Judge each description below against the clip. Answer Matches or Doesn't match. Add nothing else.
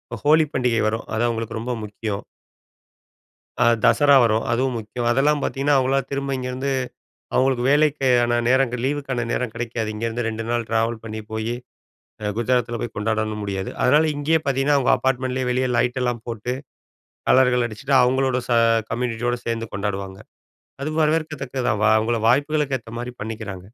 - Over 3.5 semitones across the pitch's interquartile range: Doesn't match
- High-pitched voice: Doesn't match